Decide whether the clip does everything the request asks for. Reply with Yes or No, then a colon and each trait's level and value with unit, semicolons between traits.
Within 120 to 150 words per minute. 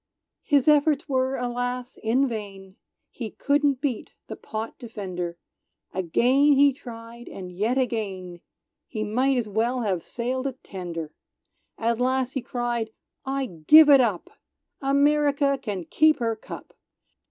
Yes: slow, 135 wpm